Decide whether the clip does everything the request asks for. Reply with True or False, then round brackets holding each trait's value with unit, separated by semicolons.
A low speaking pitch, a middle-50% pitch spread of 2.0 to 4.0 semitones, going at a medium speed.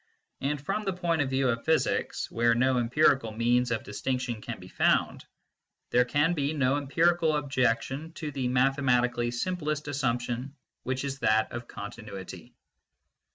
True (130 Hz; 3.6 semitones; 150 wpm)